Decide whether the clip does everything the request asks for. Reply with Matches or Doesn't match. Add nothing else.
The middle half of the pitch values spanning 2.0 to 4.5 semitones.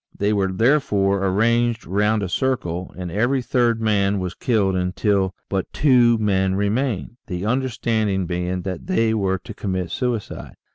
Matches